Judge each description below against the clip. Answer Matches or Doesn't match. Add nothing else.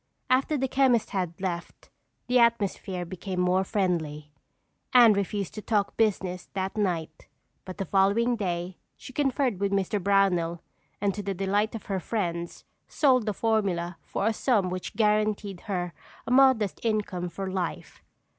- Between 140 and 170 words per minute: Matches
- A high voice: Matches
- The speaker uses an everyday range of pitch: Matches